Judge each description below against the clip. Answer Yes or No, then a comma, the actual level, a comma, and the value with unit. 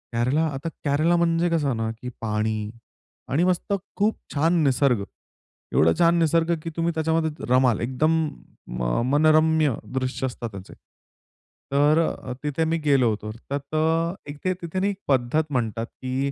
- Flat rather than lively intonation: No, average, 4.7 semitones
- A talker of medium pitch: Yes, medium, 145 Hz